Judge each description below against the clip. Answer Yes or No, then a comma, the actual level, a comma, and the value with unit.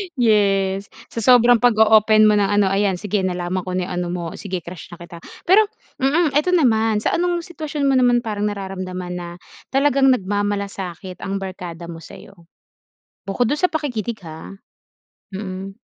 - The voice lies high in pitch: Yes, high, 205 Hz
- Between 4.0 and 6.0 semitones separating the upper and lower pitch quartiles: Yes, average, 4.7 semitones